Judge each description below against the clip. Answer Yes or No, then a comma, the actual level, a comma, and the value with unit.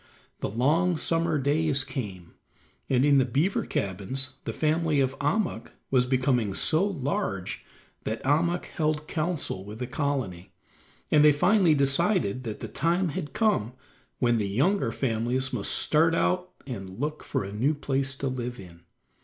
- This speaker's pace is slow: No, average, 155 wpm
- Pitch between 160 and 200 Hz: No, low, 135 Hz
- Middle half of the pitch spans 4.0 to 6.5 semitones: Yes, average, 4.9 semitones